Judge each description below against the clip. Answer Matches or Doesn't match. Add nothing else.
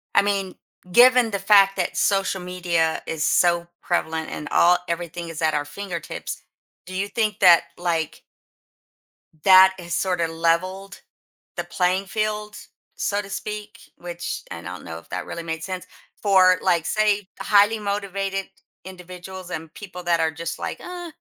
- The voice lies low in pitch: Doesn't match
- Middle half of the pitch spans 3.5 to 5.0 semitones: Doesn't match